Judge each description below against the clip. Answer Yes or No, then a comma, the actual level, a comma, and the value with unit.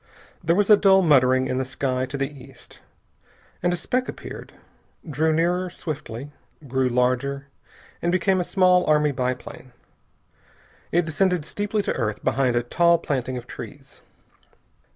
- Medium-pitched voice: Yes, medium, 145 Hz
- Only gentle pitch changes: No, wide, 5.5 semitones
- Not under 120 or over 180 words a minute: Yes, average, 150 wpm